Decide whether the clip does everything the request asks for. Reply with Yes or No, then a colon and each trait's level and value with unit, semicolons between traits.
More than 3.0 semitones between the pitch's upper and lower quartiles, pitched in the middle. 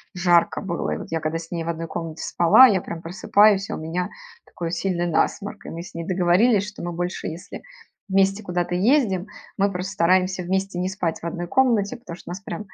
No: narrow, 2.5 semitones; medium, 180 Hz